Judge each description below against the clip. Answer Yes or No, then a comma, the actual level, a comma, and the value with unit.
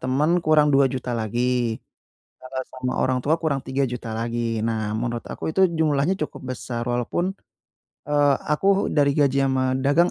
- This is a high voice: No, low, 130 Hz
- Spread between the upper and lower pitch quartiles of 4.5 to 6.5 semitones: No, average, 3.4 semitones